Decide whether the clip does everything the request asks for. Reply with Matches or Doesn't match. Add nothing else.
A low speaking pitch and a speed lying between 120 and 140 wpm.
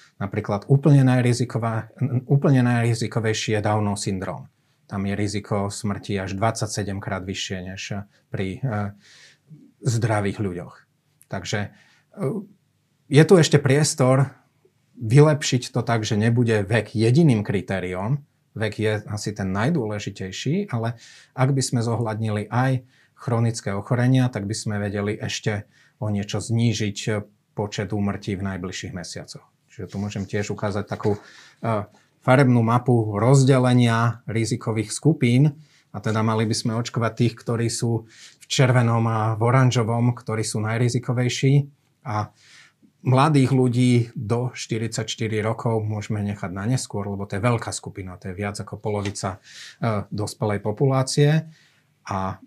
Matches